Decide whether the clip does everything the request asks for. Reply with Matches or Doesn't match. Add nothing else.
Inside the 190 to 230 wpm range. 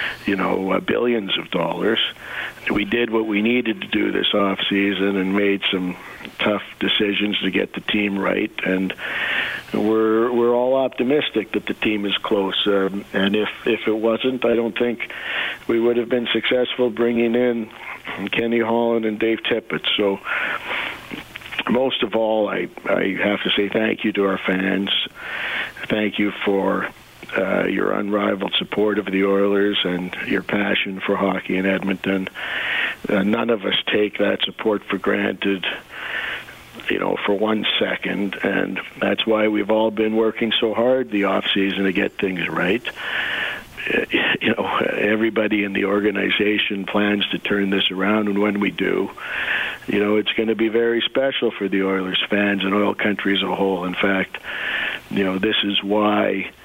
Doesn't match